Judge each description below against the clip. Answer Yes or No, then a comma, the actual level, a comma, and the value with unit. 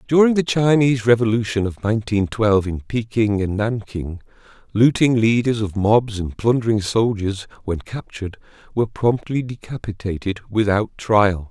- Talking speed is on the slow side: Yes, slow, 130 wpm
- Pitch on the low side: Yes, low, 110 Hz